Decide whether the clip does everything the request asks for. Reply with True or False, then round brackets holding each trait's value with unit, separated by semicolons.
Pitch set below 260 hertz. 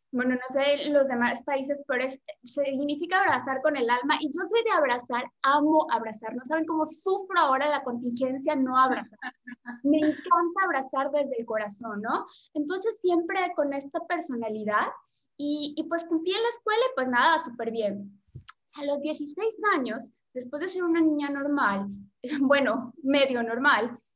False (285 Hz)